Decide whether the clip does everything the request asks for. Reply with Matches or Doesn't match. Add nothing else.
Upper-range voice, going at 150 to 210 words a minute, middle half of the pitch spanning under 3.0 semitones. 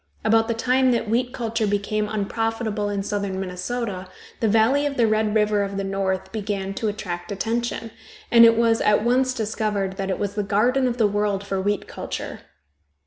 Matches